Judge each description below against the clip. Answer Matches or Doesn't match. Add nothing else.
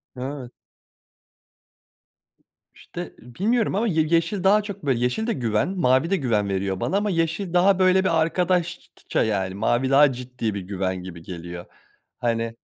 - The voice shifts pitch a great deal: Matches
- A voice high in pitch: Doesn't match